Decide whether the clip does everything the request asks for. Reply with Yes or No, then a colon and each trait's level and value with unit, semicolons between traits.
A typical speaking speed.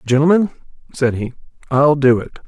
Yes: average, 145 wpm